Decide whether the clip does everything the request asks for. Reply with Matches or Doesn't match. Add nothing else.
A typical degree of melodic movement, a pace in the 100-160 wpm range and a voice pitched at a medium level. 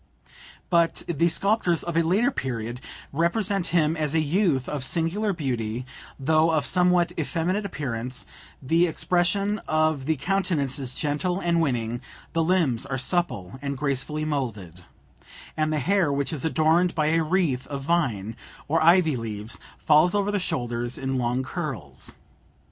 Matches